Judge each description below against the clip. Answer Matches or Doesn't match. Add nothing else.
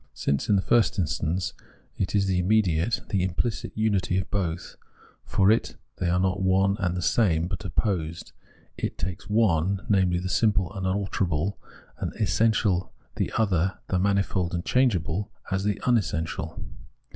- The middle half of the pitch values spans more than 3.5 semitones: Doesn't match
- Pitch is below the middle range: Matches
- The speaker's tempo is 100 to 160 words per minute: Matches